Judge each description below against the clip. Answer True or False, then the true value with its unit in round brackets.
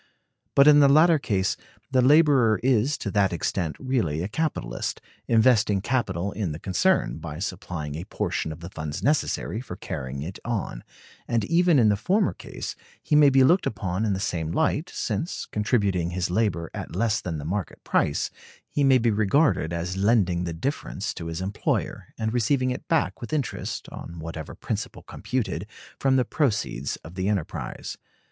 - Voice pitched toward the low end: True (105 Hz)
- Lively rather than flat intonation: True (7.1 semitones)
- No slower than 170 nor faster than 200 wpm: True (175 wpm)